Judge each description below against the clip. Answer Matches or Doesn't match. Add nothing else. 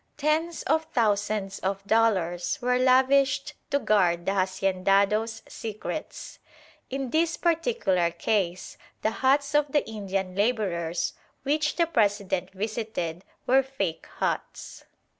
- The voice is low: Doesn't match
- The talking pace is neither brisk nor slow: Doesn't match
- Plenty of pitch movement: Matches